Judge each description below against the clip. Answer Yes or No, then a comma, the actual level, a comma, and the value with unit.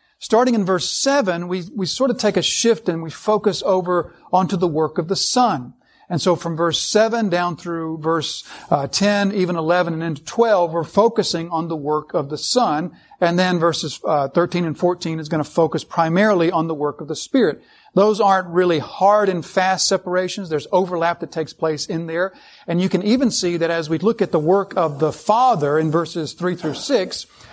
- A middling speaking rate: No, fast, 210 wpm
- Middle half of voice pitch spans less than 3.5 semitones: Yes, average, 3.0 semitones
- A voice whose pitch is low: No, medium, 175 Hz